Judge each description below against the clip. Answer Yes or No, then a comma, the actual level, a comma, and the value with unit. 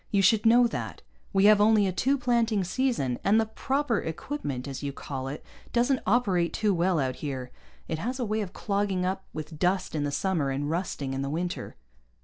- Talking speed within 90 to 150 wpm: No, fast, 205 wpm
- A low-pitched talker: No, high, 190 Hz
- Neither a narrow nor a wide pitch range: No, wide, 6.8 semitones